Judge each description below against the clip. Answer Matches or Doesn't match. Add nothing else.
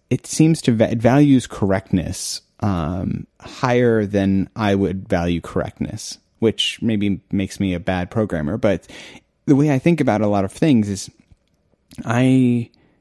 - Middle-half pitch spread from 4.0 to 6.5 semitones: Matches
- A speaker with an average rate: Matches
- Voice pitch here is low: Matches